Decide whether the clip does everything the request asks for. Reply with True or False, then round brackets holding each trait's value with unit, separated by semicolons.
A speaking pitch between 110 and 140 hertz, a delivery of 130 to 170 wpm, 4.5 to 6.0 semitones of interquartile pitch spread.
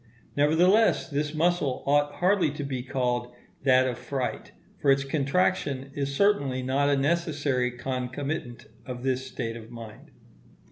False (135 Hz; 140 wpm; 2.6 semitones)